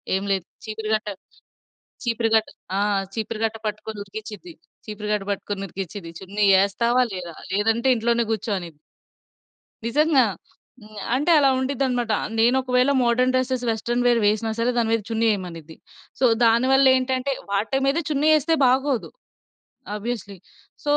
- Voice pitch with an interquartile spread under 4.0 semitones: Yes, average, 3.5 semitones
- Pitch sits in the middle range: No, high, 230 Hz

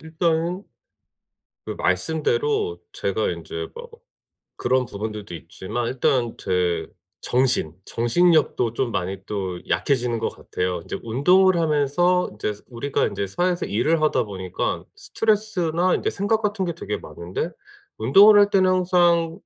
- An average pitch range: No, wide, 8.9 semitones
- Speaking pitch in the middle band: Yes, medium, 155 Hz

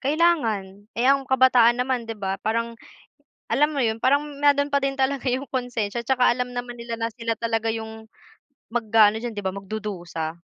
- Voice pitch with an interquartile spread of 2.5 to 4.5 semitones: Yes, average, 3.1 semitones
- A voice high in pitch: Yes, high, 235 Hz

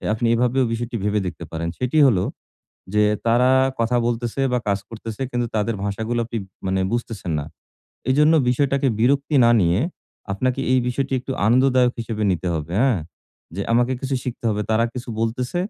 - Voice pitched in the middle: No, low, 120 Hz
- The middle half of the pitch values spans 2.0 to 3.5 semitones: Yes, average, 3.2 semitones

